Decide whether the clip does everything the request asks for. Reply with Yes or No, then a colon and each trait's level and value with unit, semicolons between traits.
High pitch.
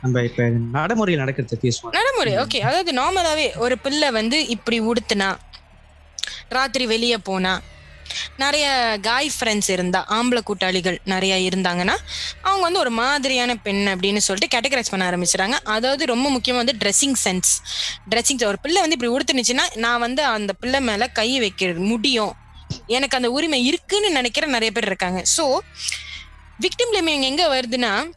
Yes: high, 235 Hz